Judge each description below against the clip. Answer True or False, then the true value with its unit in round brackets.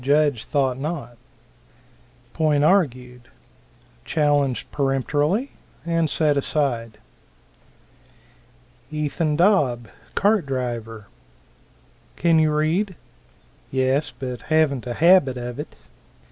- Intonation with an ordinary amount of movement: True (3.8 semitones)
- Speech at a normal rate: False (90 wpm)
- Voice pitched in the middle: True (145 Hz)